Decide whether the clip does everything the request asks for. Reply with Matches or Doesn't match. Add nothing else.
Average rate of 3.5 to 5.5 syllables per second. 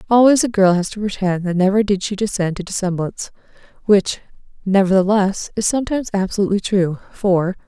Doesn't match